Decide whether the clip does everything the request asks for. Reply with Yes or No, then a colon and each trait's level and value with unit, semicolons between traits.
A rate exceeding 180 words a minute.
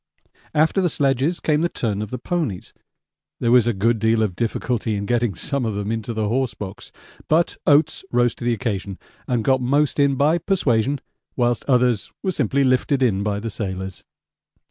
Yes: average, 190 wpm